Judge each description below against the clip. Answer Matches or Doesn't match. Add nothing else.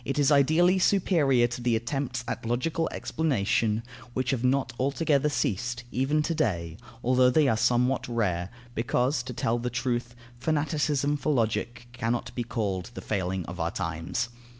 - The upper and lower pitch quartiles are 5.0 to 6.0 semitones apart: Doesn't match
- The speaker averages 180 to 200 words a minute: Doesn't match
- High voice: Doesn't match